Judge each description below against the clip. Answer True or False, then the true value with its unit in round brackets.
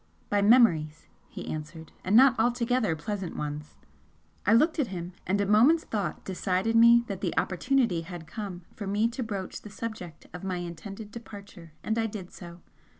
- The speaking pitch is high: True (200 Hz)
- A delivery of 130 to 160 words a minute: False (175 wpm)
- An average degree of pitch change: True (4.6 semitones)